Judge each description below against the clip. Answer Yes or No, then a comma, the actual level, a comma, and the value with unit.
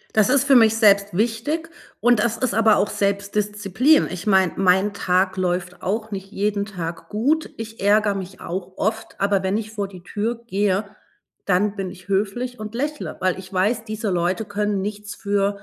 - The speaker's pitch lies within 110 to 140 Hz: No, high, 205 Hz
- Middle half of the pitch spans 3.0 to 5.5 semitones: No, narrow, 2.5 semitones